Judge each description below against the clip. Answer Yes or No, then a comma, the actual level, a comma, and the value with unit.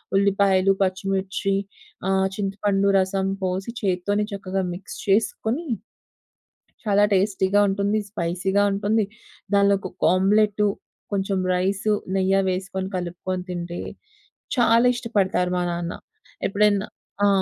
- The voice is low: No, high, 195 Hz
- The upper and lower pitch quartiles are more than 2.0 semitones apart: No, narrow, 1.5 semitones